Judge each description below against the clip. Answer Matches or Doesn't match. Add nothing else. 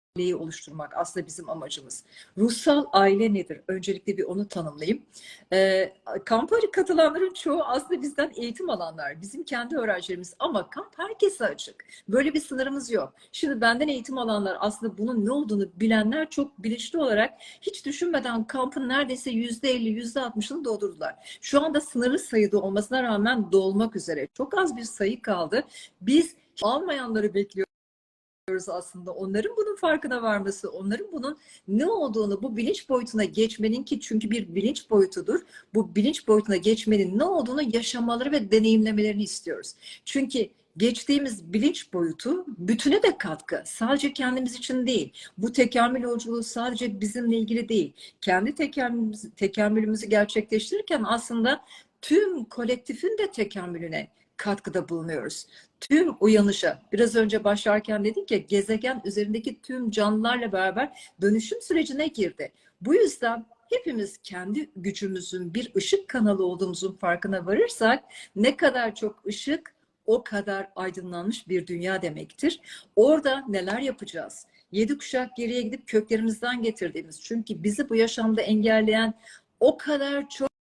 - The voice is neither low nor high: Doesn't match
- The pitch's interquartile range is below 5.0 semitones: Doesn't match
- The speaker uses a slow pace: Doesn't match